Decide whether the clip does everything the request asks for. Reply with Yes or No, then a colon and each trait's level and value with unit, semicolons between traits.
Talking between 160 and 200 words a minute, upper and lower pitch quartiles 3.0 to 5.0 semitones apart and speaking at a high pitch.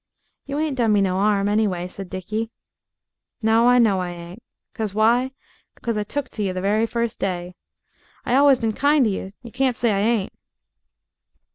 Yes: average, 185 wpm; average, 3.5 semitones; high, 215 Hz